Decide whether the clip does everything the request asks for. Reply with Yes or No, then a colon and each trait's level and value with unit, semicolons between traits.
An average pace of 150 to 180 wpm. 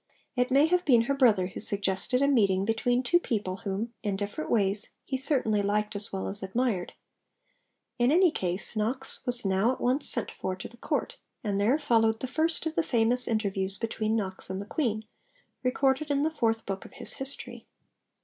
No: average, 195 wpm